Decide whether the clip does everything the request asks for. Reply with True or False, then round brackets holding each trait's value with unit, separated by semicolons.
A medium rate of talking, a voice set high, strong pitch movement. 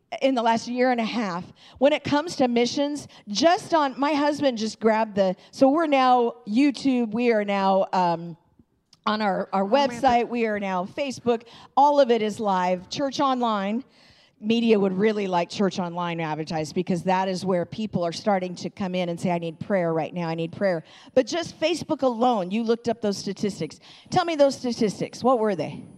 True (195 wpm; 220 Hz; 5.8 semitones)